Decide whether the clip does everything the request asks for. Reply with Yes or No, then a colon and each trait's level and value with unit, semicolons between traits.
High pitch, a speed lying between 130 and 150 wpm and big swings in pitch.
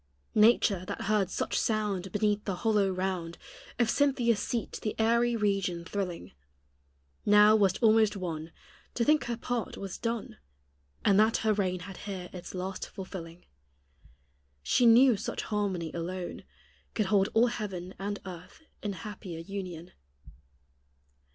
No: high, 200 Hz; average, 140 wpm; average, 3.2 semitones